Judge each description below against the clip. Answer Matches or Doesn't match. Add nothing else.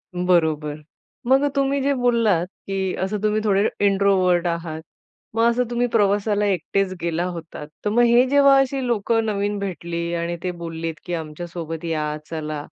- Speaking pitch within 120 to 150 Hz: Doesn't match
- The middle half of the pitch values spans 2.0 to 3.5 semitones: Doesn't match